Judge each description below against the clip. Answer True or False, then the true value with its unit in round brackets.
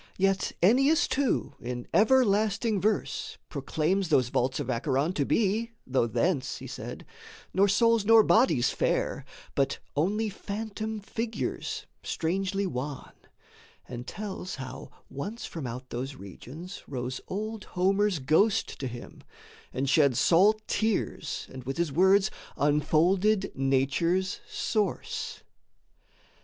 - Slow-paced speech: True (120 wpm)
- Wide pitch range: True (7.6 semitones)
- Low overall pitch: False (185 Hz)